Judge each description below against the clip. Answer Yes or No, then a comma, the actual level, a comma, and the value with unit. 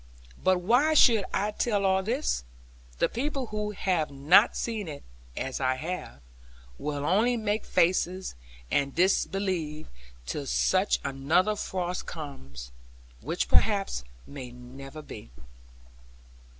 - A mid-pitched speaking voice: Yes, medium, 180 Hz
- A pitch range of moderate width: No, wide, 6.9 semitones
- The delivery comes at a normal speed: No, slow, 120 wpm